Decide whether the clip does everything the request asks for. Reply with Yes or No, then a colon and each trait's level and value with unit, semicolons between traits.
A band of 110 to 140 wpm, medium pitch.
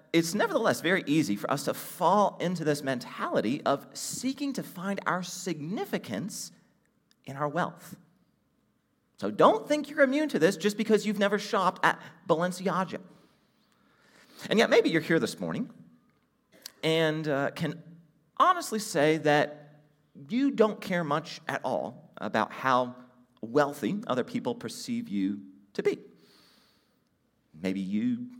Yes: slow, 135 wpm; medium, 170 Hz